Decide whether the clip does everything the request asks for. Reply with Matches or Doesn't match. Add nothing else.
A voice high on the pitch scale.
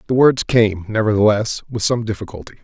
Doesn't match